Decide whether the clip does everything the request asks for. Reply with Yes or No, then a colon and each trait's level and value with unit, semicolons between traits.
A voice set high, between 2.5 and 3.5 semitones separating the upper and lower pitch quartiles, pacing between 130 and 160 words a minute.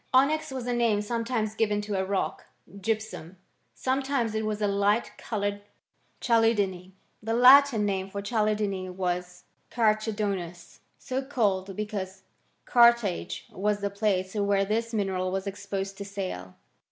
Yes: high, 205 Hz; average, 2.8 semitones; average, 140 wpm